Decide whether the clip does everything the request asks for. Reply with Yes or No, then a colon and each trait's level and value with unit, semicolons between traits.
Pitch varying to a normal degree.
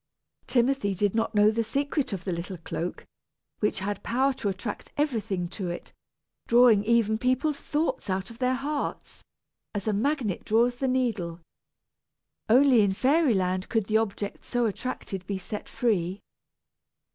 Yes: average, 4.6 semitones